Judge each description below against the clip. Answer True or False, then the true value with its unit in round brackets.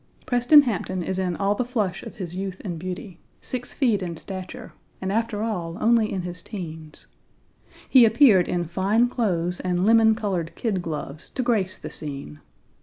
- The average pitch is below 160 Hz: False (190 Hz)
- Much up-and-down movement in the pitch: False (4.3 semitones)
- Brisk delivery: False (175 wpm)